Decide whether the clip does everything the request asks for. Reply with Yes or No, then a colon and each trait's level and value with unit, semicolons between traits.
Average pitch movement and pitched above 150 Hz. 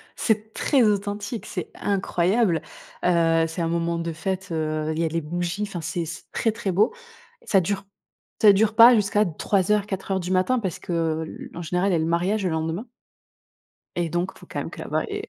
Yes: average, 3.7 semitones; medium, 185 Hz